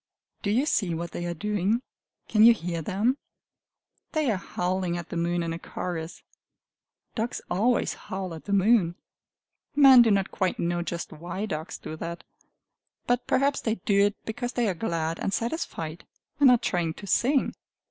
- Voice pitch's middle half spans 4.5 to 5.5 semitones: Yes, average, 5.2 semitones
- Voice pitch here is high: Yes, high, 195 Hz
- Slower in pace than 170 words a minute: No, average, 175 wpm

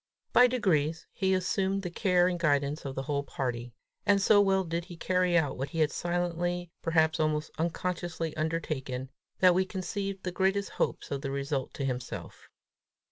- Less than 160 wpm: No, average, 175 wpm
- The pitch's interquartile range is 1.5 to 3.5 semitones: No, average, 4.3 semitones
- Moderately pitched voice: Yes, medium, 170 Hz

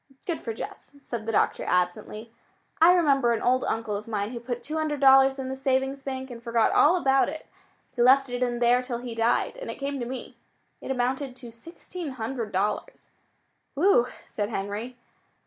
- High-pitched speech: Yes, very high, 250 Hz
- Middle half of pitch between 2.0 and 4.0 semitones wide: Yes, average, 2.9 semitones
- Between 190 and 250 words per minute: Yes, average, 195 wpm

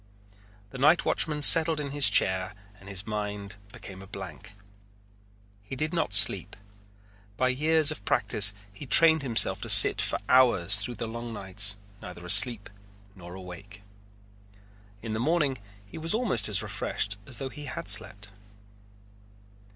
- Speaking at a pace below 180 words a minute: Yes, average, 150 wpm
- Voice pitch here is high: No, low, 110 Hz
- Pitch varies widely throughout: Yes, wide, 6.1 semitones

